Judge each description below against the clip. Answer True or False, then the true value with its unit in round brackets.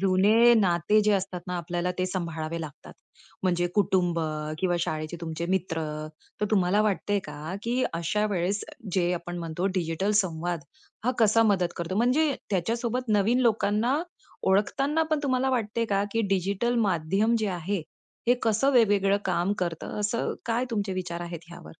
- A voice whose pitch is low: False (190 Hz)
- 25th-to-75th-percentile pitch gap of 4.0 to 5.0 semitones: True (4.3 semitones)